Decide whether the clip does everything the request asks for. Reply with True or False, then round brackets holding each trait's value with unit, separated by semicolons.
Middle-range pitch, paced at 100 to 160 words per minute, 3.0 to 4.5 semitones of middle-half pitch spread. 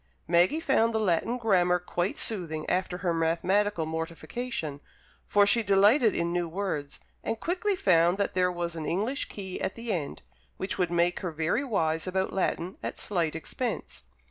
False (180 Hz; 170 wpm; 3.8 semitones)